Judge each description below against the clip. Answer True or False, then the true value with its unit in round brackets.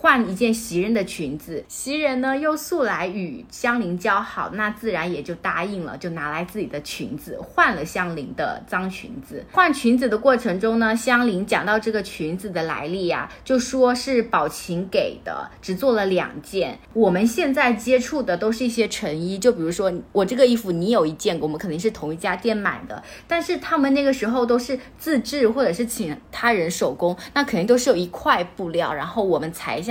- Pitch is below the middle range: False (220 Hz)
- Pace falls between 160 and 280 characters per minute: False (300 characters per minute)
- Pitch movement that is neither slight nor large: False (5.7 semitones)